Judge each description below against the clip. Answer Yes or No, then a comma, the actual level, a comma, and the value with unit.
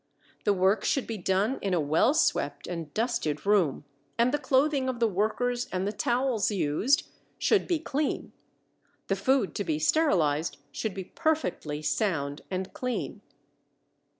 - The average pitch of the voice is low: No, high, 205 Hz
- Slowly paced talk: No, average, 150 wpm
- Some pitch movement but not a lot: No, wide, 6.8 semitones